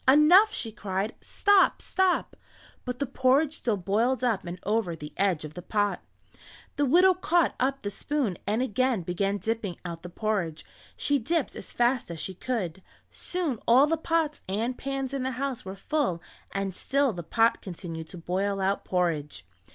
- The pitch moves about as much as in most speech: No, wide, 6.7 semitones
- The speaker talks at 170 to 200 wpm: Yes, average, 175 wpm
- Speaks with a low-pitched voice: No, high, 225 Hz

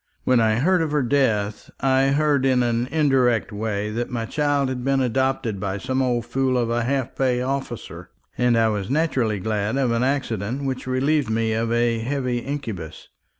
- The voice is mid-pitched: No, low, 125 Hz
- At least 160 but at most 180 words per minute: No, average, 190 wpm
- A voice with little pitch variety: No, average, 3.1 semitones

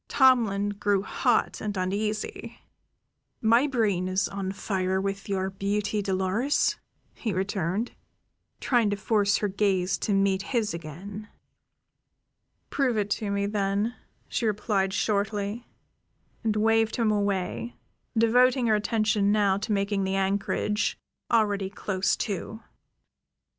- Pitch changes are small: Yes, narrow, 2.0 semitones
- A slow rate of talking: Yes, slow, 120 wpm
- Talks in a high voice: Yes, high, 205 Hz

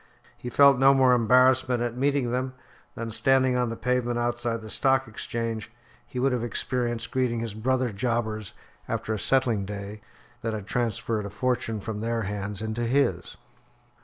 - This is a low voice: Yes, low, 120 Hz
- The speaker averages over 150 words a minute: Yes, average, 165 wpm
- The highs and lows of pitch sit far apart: No, narrow, 2.5 semitones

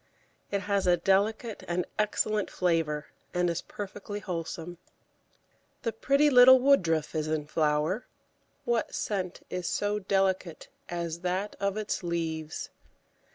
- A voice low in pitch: No, medium, 185 Hz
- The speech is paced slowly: Yes, slow, 125 wpm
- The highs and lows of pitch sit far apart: No, average, 3.8 semitones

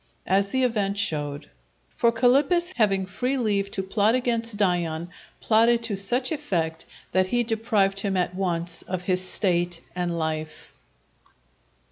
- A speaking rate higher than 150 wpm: No, average, 140 wpm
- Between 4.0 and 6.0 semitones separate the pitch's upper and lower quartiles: Yes, average, 4.7 semitones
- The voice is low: No, high, 195 Hz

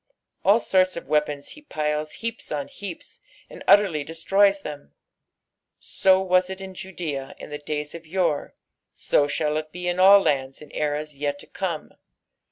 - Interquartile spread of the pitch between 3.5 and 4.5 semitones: Yes, average, 4.2 semitones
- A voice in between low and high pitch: Yes, medium, 160 Hz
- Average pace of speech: Yes, average, 170 wpm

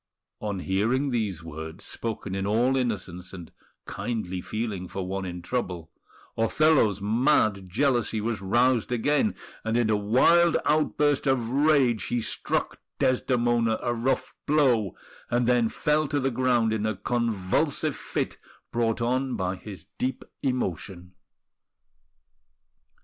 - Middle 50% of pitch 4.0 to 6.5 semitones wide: Yes, average, 4.8 semitones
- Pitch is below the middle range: Yes, low, 115 Hz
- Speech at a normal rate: No, slow, 130 wpm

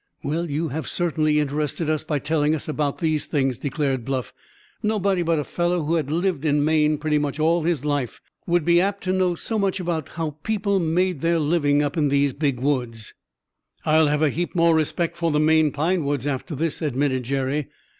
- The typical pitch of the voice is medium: Yes, medium, 155 Hz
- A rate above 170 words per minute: Yes, average, 200 wpm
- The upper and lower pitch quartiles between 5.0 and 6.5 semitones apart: No, average, 2.8 semitones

